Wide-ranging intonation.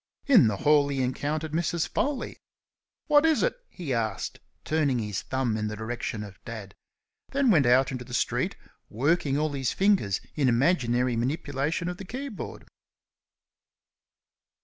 Yes: wide, 6.3 semitones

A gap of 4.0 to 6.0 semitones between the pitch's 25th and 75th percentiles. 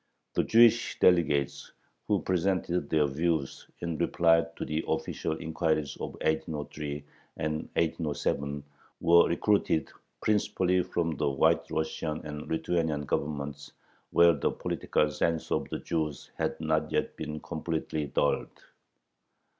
No: narrow, 2.4 semitones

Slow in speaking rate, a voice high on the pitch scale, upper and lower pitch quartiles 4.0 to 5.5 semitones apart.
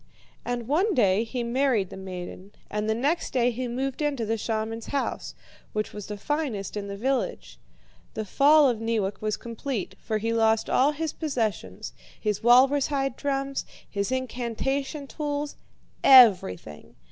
No: average, 155 wpm; high, 235 Hz; average, 4.4 semitones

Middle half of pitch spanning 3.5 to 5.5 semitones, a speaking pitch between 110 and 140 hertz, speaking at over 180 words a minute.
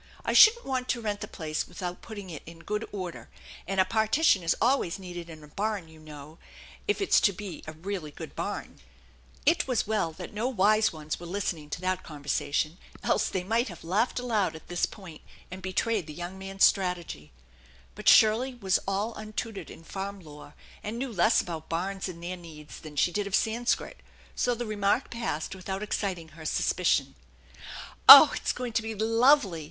No: average, 4.6 semitones; high, 195 Hz; average, 195 wpm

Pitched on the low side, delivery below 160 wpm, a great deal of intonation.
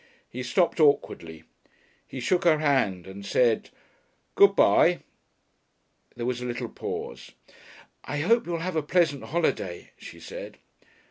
No: medium, 145 Hz; average, 140 wpm; wide, 6.4 semitones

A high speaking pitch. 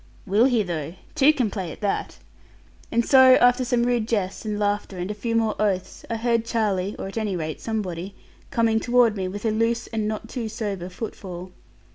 Yes: high, 215 Hz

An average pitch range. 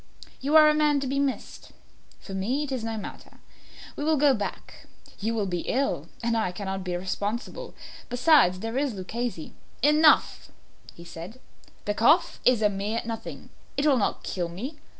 No: wide, 6.2 semitones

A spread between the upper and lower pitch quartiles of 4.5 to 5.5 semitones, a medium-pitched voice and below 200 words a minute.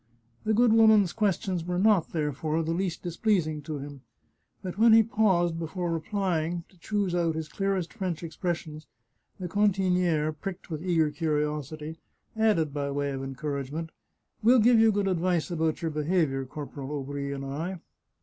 No: average, 4.1 semitones; medium, 165 Hz; average, 160 wpm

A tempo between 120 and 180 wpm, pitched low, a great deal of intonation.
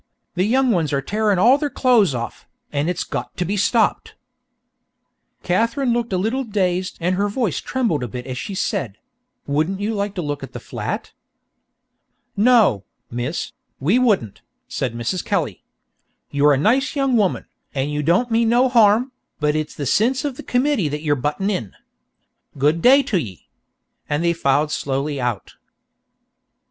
No: average, 170 wpm; medium, 185 Hz; wide, 7.9 semitones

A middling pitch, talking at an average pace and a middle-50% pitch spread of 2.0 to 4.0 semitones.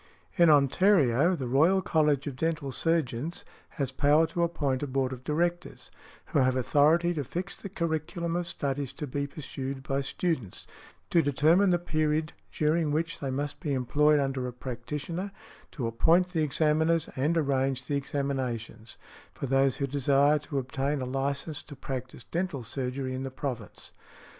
Yes: medium, 145 Hz; average, 160 wpm; average, 3.5 semitones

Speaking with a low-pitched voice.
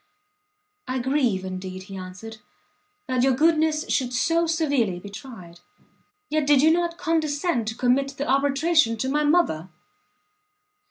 No: very high, 270 Hz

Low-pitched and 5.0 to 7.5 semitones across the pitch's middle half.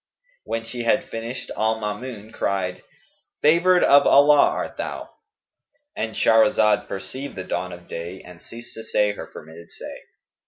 Yes: low, 110 Hz; wide, 5.5 semitones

